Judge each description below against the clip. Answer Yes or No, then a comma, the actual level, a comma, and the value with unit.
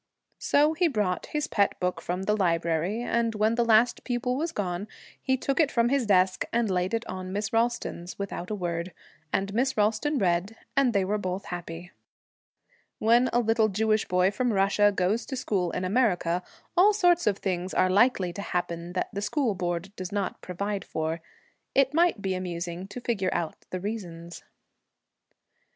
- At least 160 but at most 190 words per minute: Yes, average, 180 wpm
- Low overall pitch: No, high, 200 Hz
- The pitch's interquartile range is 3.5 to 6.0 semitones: Yes, average, 4.5 semitones